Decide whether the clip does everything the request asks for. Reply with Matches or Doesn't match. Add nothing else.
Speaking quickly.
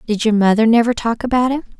Matches